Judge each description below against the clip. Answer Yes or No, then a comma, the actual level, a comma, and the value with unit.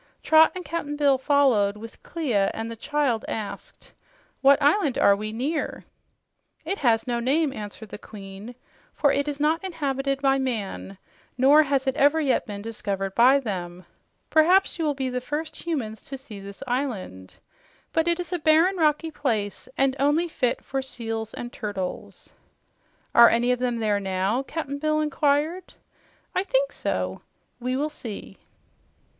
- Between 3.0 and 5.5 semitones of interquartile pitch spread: Yes, average, 5.2 semitones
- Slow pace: No, average, 160 wpm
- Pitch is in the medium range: No, very high, 270 Hz